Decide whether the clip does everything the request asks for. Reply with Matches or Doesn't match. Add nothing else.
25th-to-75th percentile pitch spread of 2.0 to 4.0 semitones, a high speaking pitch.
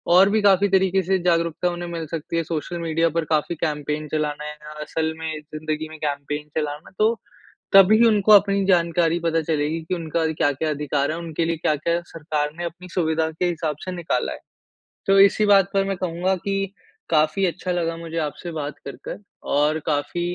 Doesn't match